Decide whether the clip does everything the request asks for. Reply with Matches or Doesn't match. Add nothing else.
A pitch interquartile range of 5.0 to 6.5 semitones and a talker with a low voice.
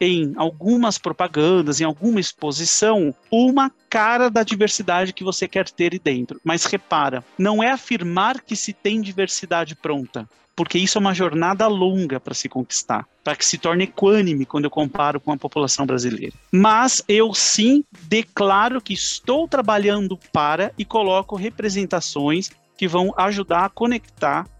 Doesn't match